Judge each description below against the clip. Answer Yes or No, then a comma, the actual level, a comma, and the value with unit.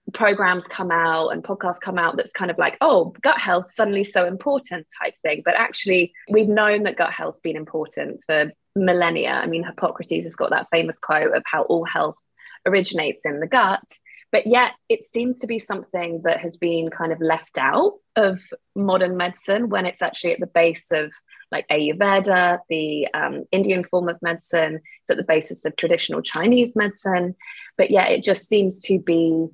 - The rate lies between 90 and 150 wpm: No, average, 190 wpm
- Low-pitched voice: No, medium, 180 Hz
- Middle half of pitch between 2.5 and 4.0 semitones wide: Yes, average, 3.3 semitones